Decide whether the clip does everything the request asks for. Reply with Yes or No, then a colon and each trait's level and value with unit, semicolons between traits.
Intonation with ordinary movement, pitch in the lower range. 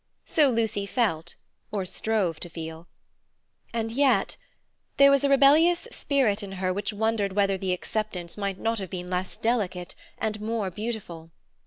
No: average, 3.9 semitones; high, 205 Hz